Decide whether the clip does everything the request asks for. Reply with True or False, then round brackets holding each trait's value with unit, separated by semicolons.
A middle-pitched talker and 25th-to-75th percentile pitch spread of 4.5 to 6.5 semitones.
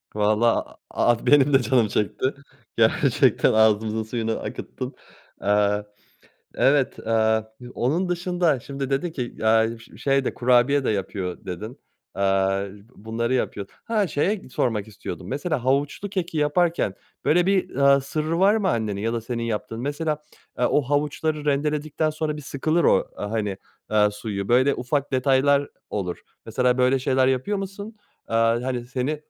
False (130 Hz; 5.1 semitones)